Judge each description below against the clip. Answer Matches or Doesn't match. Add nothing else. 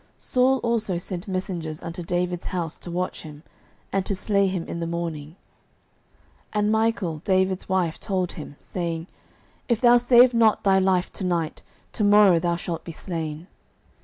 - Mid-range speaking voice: Matches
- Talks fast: Doesn't match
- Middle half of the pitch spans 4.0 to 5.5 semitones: Doesn't match